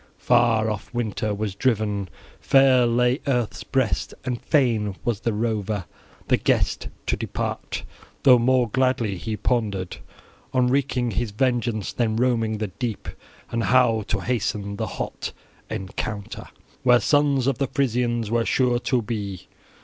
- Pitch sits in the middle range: No, low, 115 Hz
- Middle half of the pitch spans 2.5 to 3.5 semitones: Yes, average, 2.9 semitones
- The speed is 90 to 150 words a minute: Yes, average, 140 wpm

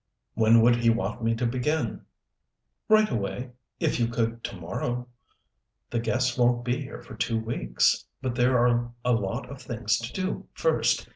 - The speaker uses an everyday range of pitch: No, narrow, 1.6 semitones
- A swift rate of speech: No, average, 170 wpm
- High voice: No, low, 120 Hz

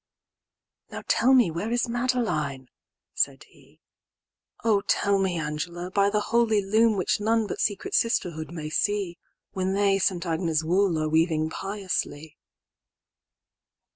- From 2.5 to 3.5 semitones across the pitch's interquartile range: No, average, 4.6 semitones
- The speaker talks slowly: Yes, slow, 120 wpm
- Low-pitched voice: No, high, 190 Hz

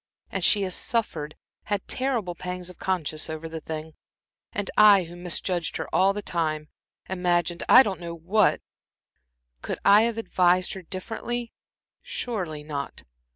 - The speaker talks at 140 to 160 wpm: Yes, average, 150 wpm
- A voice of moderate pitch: Yes, medium, 180 Hz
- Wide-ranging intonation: No, average, 3.8 semitones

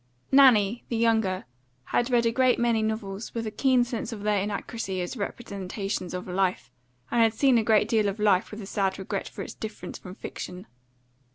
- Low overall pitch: No, high, 215 Hz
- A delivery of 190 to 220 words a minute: Yes, average, 195 wpm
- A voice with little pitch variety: No, average, 3.0 semitones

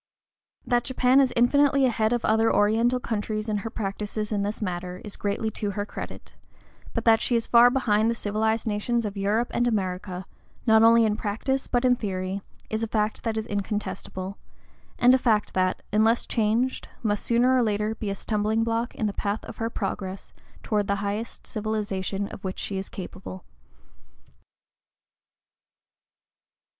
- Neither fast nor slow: Yes, average, 170 wpm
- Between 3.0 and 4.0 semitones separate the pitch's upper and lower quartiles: No, narrow, 2.4 semitones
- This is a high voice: Yes, high, 215 Hz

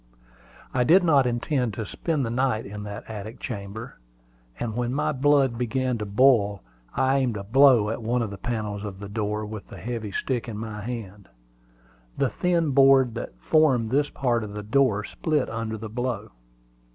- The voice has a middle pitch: No, low, 115 Hz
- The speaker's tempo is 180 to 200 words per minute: Yes, average, 185 wpm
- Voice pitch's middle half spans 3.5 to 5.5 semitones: Yes, average, 3.9 semitones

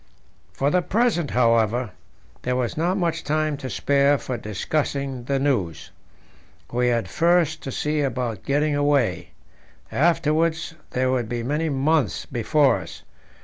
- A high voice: No, medium, 140 Hz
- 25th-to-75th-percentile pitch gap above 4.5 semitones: No, average, 4.0 semitones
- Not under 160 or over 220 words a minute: No, average, 140 wpm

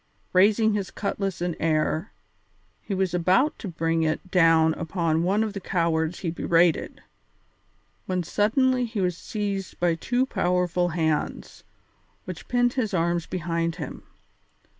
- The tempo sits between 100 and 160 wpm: Yes, average, 140 wpm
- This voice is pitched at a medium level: Yes, medium, 180 Hz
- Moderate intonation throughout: Yes, average, 3.5 semitones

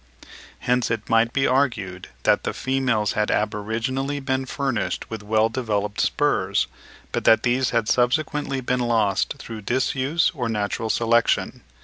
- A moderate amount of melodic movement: Yes, average, 3.4 semitones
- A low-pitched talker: Yes, low, 120 Hz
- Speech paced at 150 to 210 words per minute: No, average, 140 wpm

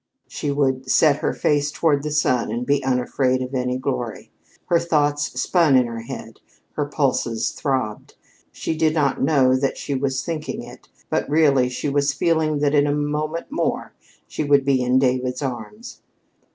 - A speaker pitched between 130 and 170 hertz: Yes, medium, 140 Hz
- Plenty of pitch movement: No, narrow, 2.6 semitones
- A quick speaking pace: No, average, 175 wpm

